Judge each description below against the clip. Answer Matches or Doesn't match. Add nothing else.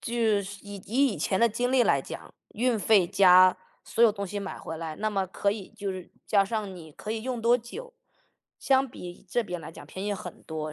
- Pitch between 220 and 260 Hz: Doesn't match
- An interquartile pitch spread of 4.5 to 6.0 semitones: Doesn't match